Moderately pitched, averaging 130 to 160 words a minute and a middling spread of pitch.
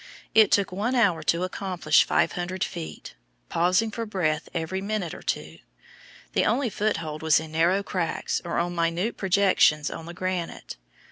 Yes: medium, 180 Hz; average, 155 wpm; average, 3.5 semitones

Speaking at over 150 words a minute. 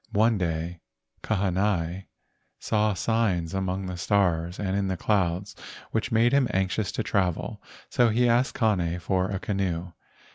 No: average, 145 wpm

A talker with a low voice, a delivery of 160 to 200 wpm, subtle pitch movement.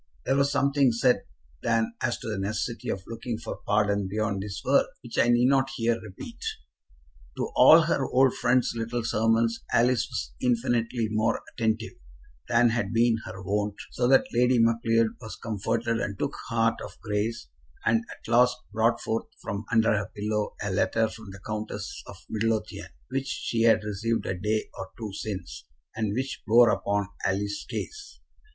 Yes: low, 115 Hz; average, 170 wpm; narrow, 2.2 semitones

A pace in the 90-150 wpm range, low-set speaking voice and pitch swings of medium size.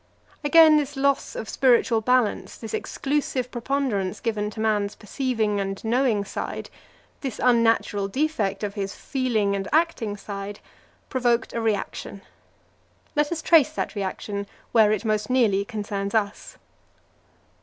No: slow, 135 wpm; high, 225 Hz; average, 4.3 semitones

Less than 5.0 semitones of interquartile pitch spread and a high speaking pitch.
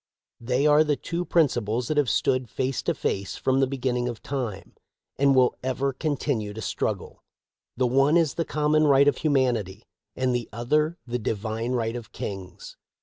No: average, 3.7 semitones; low, 130 Hz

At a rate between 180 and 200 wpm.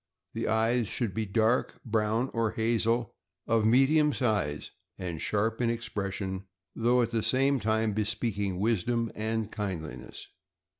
No: average, 140 wpm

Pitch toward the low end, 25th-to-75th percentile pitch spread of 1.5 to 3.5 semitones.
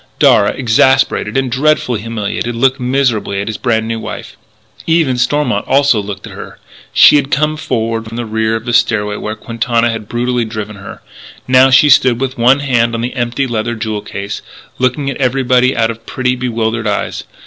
Yes: low, 120 Hz; average, 2.8 semitones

